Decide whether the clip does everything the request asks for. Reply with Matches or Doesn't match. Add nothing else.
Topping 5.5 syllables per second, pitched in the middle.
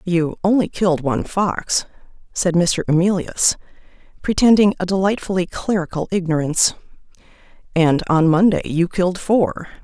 Doesn't match